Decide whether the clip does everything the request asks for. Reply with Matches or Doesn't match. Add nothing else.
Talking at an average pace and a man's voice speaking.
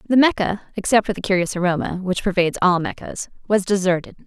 Doesn't match